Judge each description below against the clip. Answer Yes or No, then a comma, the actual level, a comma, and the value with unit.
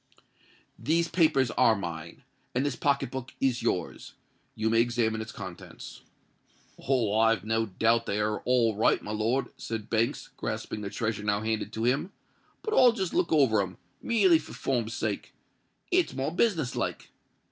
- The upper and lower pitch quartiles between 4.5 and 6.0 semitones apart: No, average, 4.1 semitones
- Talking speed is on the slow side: No, average, 160 wpm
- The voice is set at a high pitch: No, low, 115 Hz